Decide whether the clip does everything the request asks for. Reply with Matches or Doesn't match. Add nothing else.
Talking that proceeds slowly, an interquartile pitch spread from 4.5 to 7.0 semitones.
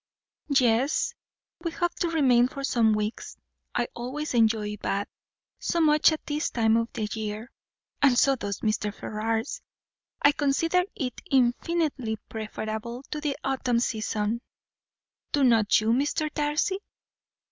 Matches